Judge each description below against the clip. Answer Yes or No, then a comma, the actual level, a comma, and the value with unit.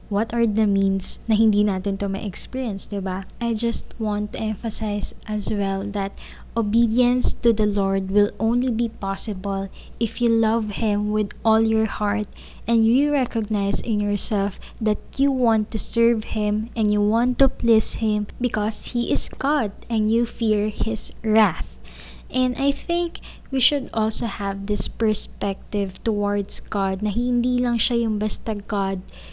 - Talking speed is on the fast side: Yes, fast, 165 wpm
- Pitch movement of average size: No, narrow, 2.3 semitones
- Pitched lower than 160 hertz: No, high, 215 Hz